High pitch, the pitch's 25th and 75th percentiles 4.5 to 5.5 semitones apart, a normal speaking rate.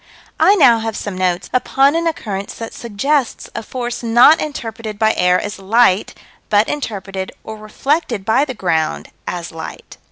Yes: high, 220 Hz; average, 4.9 semitones; average, 160 wpm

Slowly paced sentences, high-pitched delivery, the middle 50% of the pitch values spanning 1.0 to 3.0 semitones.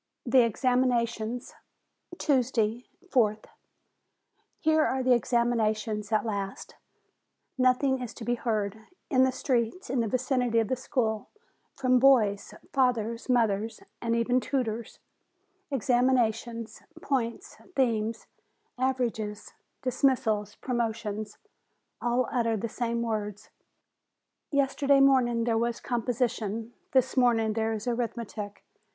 Yes: slow, 110 wpm; high, 235 Hz; narrow, 2.5 semitones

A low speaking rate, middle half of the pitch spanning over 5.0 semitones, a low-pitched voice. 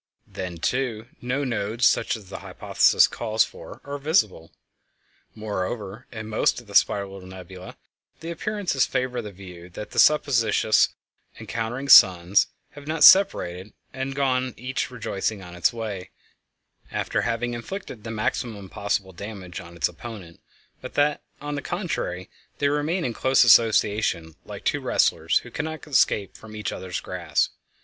No: average, 150 wpm; wide, 5.6 semitones; low, 110 Hz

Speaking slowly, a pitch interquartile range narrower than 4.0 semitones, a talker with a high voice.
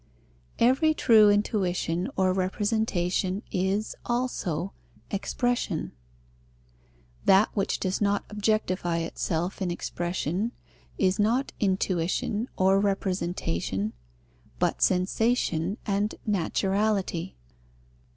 Yes: slow, 85 wpm; average, 2.9 semitones; high, 195 Hz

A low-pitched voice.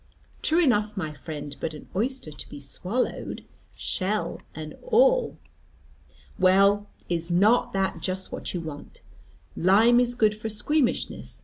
No: high, 200 Hz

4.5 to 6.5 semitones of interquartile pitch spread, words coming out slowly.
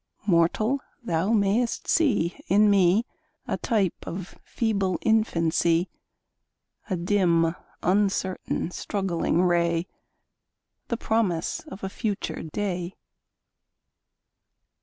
No: average, 3.7 semitones; slow, 90 wpm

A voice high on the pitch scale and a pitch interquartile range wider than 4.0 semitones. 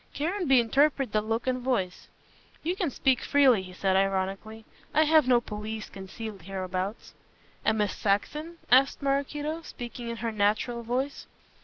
Yes: high, 235 Hz; average, 5.1 semitones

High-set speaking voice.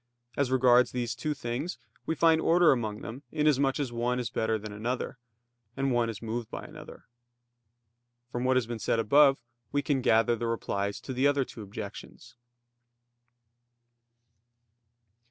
No: low, 125 Hz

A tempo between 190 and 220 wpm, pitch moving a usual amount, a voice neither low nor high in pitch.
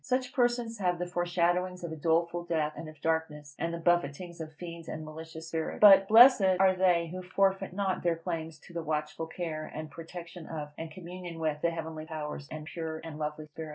No: fast, 205 wpm; narrow, 2.3 semitones; medium, 165 Hz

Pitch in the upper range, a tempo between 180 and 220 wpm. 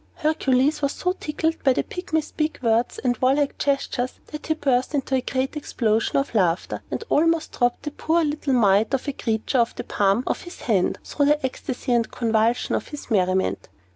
Yes: very high, 265 Hz; average, 195 wpm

